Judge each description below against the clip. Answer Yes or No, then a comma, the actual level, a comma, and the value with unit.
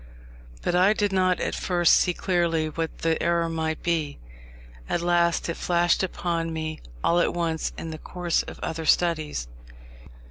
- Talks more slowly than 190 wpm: Yes, average, 165 wpm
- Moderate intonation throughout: No, narrow, 1.5 semitones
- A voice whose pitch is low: No, medium, 170 Hz